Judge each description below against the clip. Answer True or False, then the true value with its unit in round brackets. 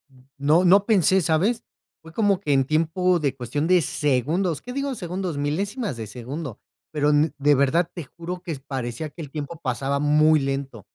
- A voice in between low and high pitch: True (155 Hz)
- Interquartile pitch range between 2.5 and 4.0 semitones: False (4.4 semitones)